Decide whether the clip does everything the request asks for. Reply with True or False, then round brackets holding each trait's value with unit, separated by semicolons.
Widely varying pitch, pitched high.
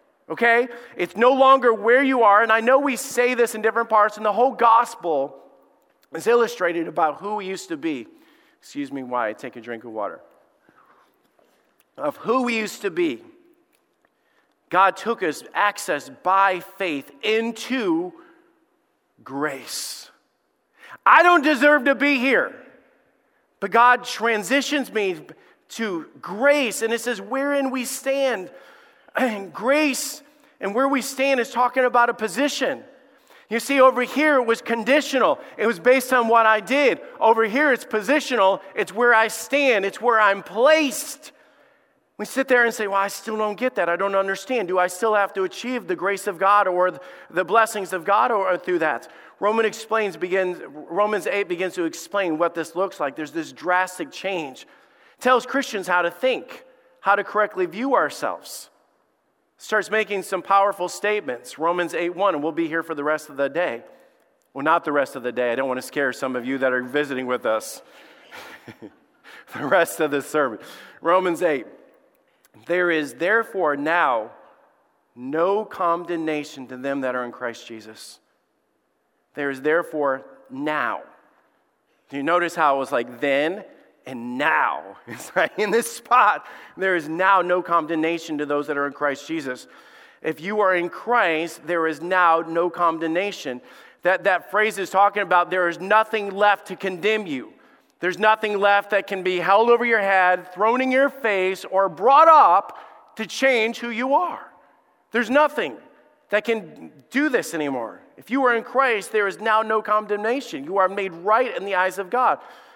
True (6.4 semitones; 210 Hz)